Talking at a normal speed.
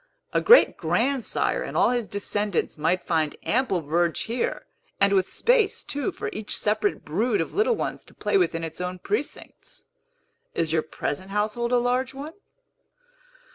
Yes: average, 160 wpm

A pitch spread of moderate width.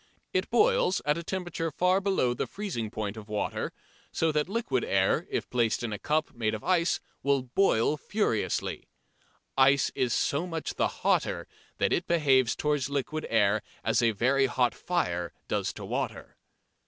No: wide, 6.4 semitones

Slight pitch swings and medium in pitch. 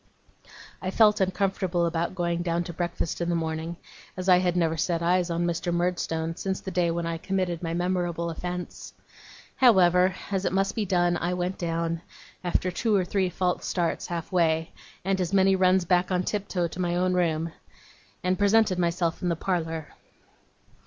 Yes: narrow, 1.7 semitones; medium, 175 Hz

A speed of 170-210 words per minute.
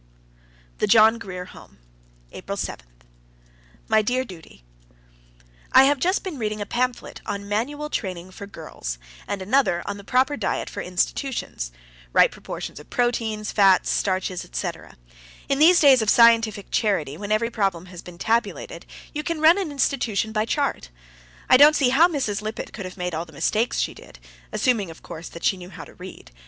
Yes: average, 175 wpm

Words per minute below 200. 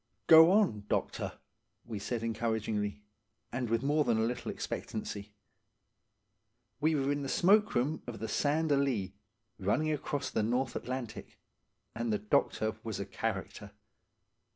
Yes: average, 145 wpm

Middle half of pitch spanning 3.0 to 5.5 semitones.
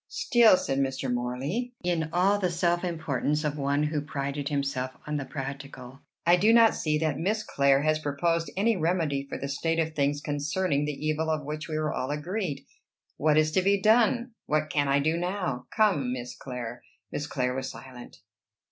Yes: average, 4.0 semitones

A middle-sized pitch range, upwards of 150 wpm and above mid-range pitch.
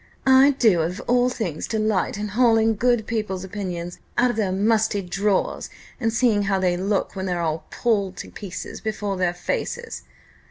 Yes: average, 3.3 semitones; average, 170 wpm; high, 205 Hz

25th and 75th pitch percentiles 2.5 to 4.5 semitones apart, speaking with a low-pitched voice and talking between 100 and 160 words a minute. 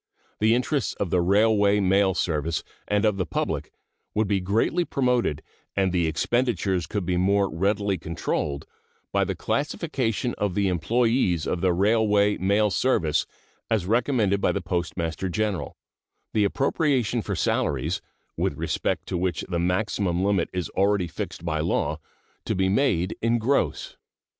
Yes: average, 3.8 semitones; low, 100 Hz; average, 150 wpm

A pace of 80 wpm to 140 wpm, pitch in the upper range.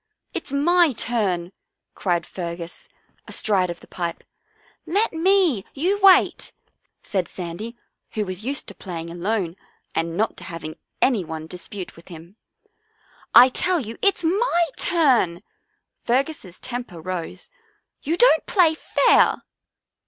Yes: slow, 135 wpm; high, 215 Hz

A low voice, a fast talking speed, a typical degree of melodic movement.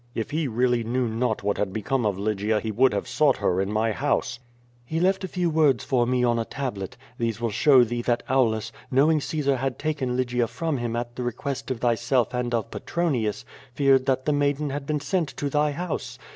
Yes: low, 125 Hz; fast, 215 wpm; average, 3.7 semitones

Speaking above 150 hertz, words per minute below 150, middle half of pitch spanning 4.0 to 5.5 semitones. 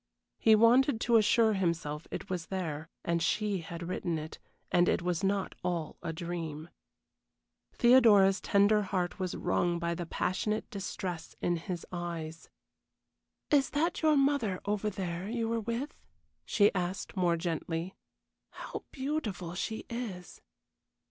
Yes: medium, 185 Hz; average, 140 wpm; average, 4.3 semitones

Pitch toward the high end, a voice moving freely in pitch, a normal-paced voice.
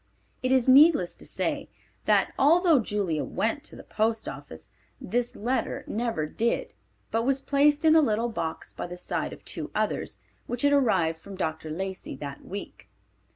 Yes: high, 225 Hz; wide, 7.2 semitones; average, 170 wpm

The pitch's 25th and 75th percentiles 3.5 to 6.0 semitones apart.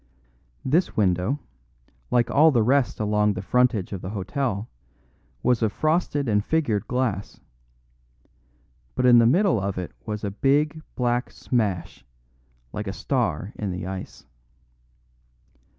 Yes: average, 5.1 semitones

